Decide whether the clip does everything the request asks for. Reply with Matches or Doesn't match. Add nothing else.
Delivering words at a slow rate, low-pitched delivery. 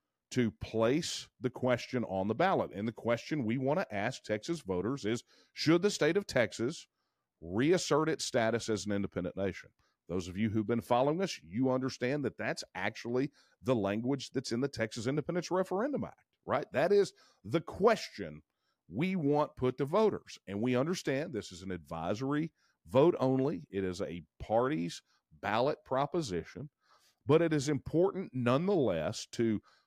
Doesn't match